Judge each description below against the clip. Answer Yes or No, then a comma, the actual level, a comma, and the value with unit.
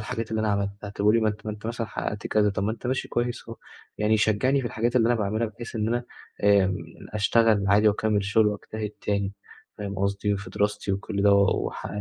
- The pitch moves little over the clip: Yes, narrow, 1.9 semitones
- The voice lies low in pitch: Yes, low, 105 Hz